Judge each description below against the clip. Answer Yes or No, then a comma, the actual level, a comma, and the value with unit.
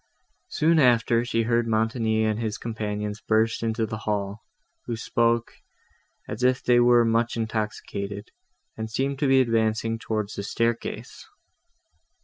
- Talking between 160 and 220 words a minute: No, slow, 135 wpm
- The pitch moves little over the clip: Yes, narrow, 1.3 semitones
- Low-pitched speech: Yes, low, 115 Hz